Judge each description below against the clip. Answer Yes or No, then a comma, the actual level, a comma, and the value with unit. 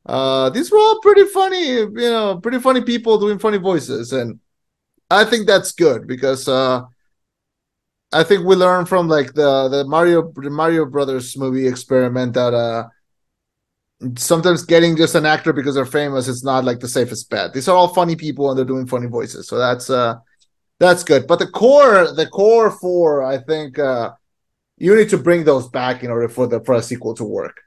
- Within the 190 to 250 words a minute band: Yes, average, 195 wpm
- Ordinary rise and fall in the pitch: No, wide, 6.3 semitones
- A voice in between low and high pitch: Yes, medium, 150 Hz